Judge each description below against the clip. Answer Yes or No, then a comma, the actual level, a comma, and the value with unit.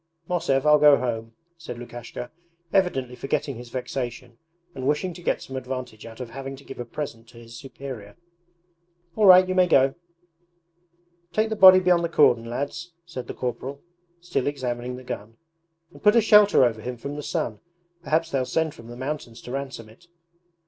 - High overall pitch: No, low, 135 Hz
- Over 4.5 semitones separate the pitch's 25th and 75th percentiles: Yes, average, 5.1 semitones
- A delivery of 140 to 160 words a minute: No, average, 185 wpm